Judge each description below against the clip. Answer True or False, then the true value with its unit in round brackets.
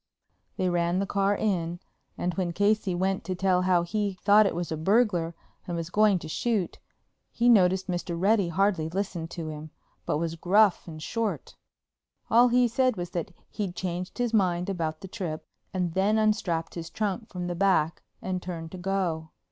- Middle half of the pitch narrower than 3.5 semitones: True (3.1 semitones)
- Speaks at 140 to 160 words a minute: False (190 wpm)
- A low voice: False (185 Hz)